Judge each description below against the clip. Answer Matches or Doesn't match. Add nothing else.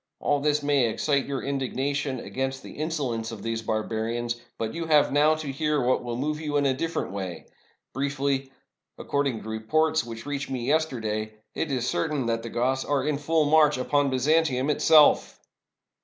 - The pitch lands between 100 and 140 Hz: Matches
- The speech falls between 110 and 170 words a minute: Doesn't match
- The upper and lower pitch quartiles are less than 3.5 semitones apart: Doesn't match